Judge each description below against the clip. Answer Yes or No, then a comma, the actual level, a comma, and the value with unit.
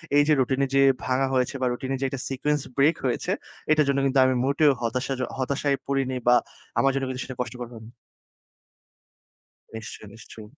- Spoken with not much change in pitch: Yes, narrow, 1.6 semitones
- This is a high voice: No, low, 135 Hz